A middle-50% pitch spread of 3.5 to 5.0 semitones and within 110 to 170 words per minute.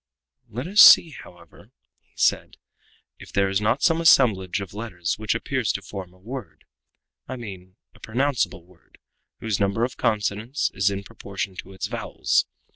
Yes: average, 4.2 semitones; average, 165 wpm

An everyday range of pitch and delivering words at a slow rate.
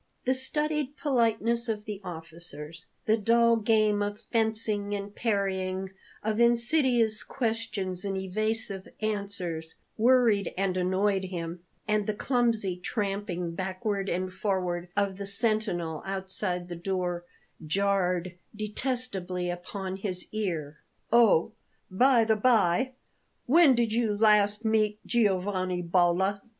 Yes: average, 3.4 semitones; slow, 115 wpm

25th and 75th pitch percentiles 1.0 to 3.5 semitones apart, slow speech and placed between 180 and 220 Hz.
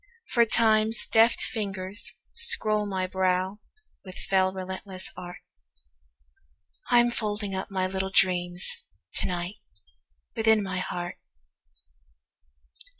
Yes: average, 2.9 semitones; slow, 90 wpm; high, 190 Hz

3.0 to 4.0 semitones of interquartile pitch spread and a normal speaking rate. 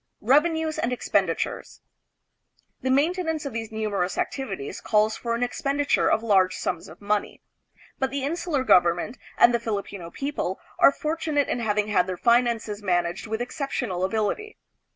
No: wide, 5.6 semitones; average, 150 wpm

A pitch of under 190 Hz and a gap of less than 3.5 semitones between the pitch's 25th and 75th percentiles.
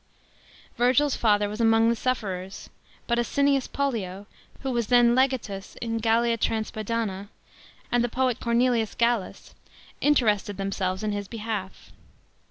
No: high, 230 Hz; average, 2.9 semitones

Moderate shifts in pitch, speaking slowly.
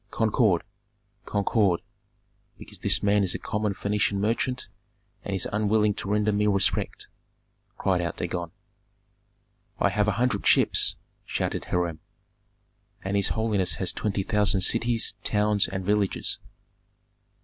No: narrow, 1.7 semitones; slow, 125 wpm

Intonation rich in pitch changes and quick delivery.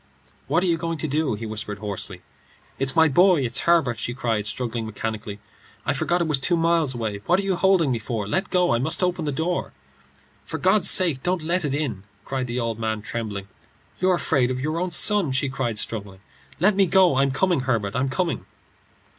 Yes: wide, 7.0 semitones; fast, 210 wpm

